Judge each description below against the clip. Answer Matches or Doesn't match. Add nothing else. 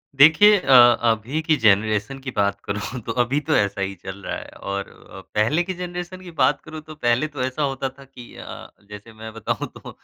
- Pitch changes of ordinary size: Doesn't match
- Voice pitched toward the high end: Doesn't match